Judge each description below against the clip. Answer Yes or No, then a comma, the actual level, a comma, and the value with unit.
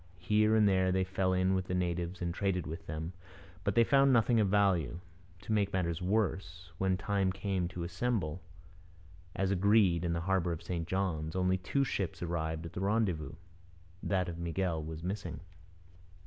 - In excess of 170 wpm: Yes, average, 180 wpm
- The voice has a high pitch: No, very low, 95 Hz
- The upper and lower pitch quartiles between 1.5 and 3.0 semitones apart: Yes, average, 2.7 semitones